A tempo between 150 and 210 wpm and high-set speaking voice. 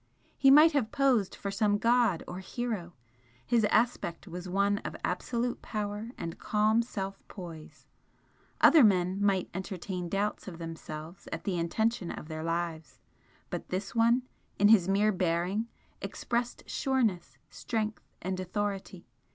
No: average, 140 wpm; high, 200 Hz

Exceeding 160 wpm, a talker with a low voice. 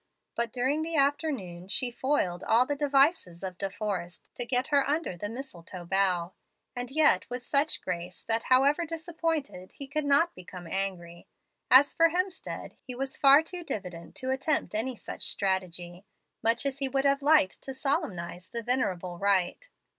No: average, 170 wpm; very high, 250 Hz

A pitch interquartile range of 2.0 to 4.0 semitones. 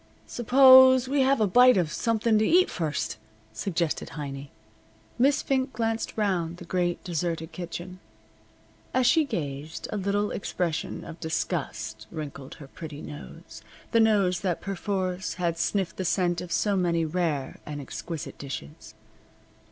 No: wide, 5.4 semitones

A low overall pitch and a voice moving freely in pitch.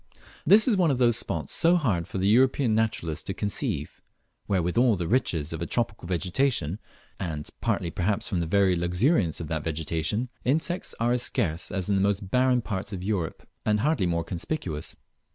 Yes: low, 100 Hz; wide, 6.3 semitones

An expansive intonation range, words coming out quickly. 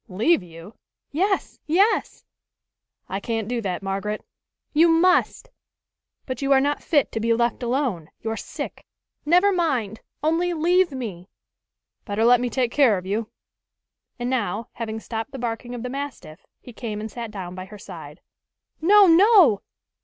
No: wide, 6.5 semitones; average, 160 wpm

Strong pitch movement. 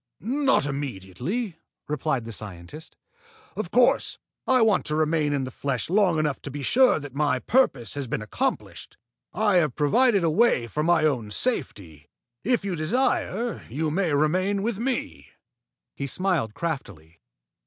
Yes: wide, 7.3 semitones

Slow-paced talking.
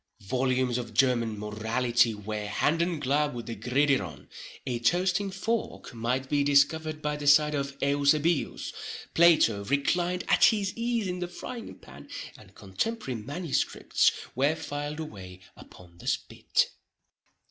Yes: slow, 125 wpm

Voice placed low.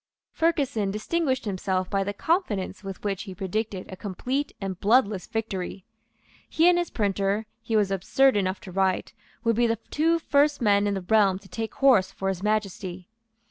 No: high, 205 Hz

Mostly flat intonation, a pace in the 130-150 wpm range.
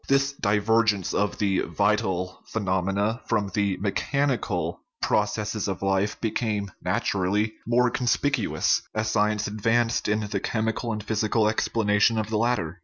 Yes: narrow, 2.1 semitones; slow, 135 wpm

